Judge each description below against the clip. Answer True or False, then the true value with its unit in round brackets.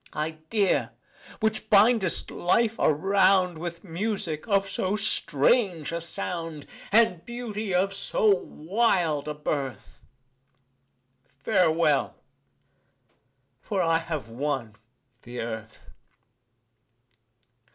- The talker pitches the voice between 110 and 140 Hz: False (175 Hz)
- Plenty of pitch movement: False (4.8 semitones)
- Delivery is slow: True (90 wpm)